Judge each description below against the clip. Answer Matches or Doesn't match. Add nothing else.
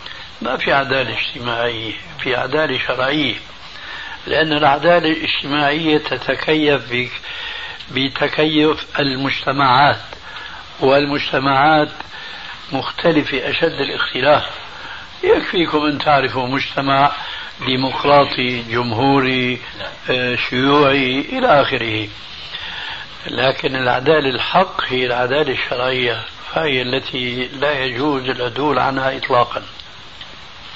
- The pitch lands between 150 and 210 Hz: Doesn't match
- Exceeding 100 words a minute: Doesn't match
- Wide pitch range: Doesn't match